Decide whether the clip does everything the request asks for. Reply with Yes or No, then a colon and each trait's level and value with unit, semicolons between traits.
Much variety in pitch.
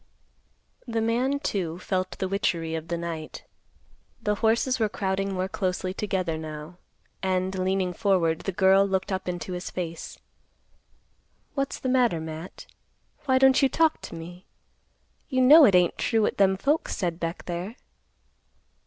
No: average, 4.4 semitones